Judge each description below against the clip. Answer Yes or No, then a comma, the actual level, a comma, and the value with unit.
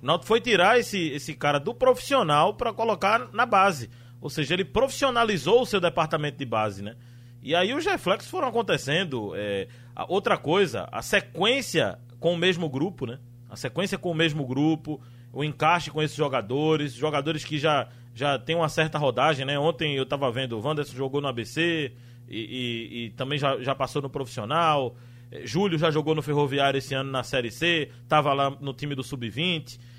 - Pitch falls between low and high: Yes, medium, 145 Hz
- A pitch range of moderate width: Yes, average, 4.7 semitones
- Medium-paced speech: No, fast, 190 wpm